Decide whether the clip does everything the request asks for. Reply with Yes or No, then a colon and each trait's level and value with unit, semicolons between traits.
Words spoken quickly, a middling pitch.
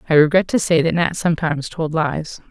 Yes: fast, 215 wpm; medium, 160 Hz